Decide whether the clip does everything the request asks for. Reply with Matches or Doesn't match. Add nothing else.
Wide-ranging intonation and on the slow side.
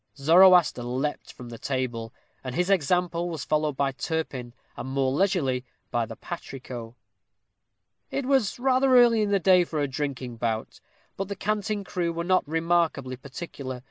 Doesn't match